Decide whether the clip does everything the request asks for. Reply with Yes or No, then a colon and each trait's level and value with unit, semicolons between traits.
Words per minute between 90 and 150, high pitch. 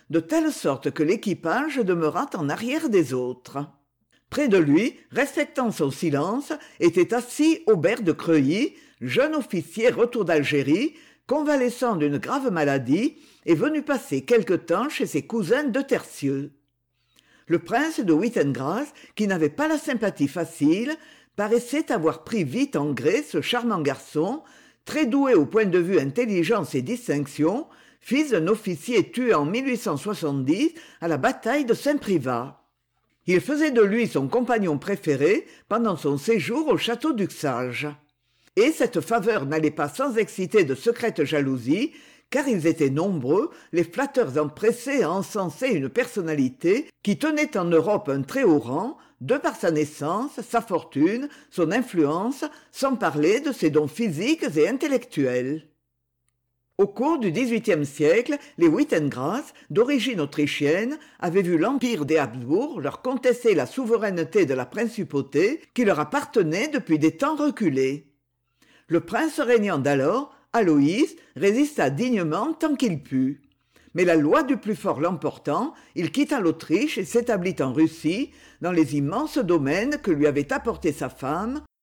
Yes: slow, 145 wpm; high, 210 Hz